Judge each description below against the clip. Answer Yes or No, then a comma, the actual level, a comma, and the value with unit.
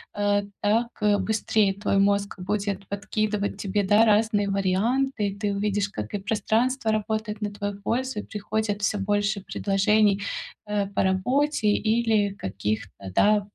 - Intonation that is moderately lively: No, narrow, 1.5 semitones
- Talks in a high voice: Yes, high, 205 Hz